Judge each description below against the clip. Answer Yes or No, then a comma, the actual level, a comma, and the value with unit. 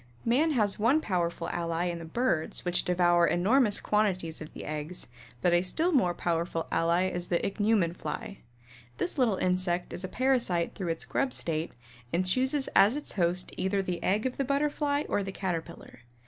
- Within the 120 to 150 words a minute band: No, average, 180 wpm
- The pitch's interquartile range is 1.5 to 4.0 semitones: No, wide, 5.5 semitones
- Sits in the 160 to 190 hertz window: Yes, medium, 185 Hz